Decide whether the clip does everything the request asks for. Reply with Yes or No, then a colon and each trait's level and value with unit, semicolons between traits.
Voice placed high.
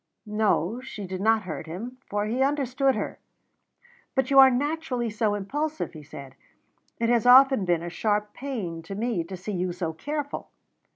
Yes: high, 215 Hz